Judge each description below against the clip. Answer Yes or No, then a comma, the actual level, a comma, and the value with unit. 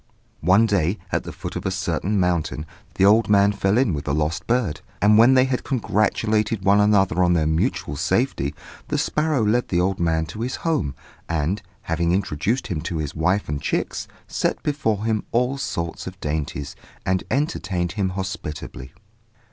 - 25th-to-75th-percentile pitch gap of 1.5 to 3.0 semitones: No, average, 5.2 semitones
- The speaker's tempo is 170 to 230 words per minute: Yes, average, 180 wpm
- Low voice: Yes, very low, 95 Hz